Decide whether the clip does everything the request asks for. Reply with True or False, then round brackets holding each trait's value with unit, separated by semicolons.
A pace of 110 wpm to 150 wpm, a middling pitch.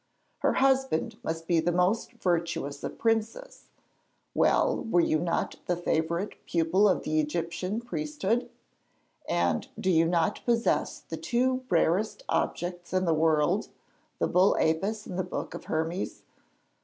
True (145 wpm; 175 Hz)